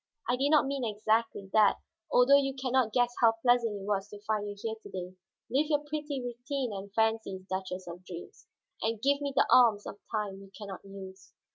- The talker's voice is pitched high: Yes, high, 220 Hz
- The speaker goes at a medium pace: No, fast, 215 wpm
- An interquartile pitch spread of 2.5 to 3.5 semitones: No, average, 4.6 semitones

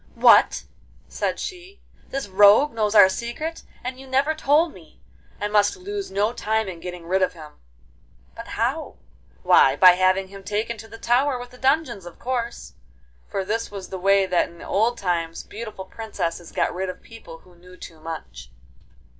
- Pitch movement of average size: Yes, average, 5.0 semitones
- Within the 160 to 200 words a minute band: Yes, average, 180 wpm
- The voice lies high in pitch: Yes, high, 205 Hz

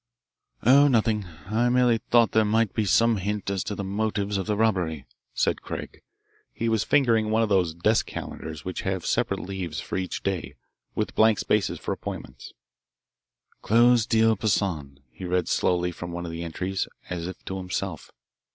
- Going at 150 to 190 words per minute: Yes, average, 175 wpm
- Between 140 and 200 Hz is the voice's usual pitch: No, low, 100 Hz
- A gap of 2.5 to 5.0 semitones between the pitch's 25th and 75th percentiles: Yes, average, 3.8 semitones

